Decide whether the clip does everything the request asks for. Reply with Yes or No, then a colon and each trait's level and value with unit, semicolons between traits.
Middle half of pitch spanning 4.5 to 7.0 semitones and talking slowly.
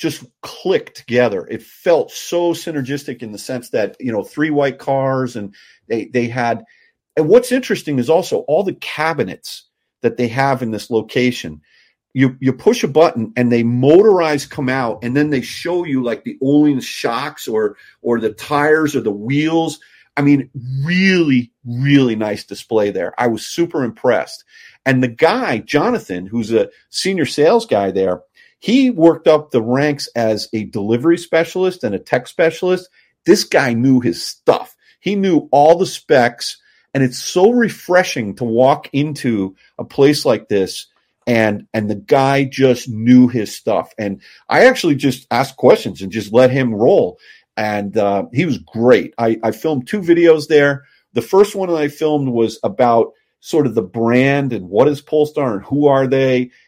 No: average, 5.1 semitones; average, 175 wpm